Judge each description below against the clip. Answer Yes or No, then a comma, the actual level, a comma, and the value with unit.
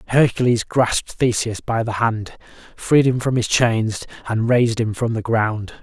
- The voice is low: Yes, low, 115 Hz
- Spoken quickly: No, average, 175 wpm